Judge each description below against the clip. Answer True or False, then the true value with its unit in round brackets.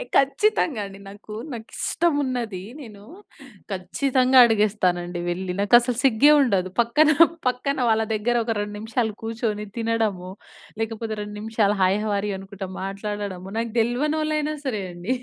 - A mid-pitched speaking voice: False (220 Hz)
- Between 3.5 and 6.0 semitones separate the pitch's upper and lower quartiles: True (3.8 semitones)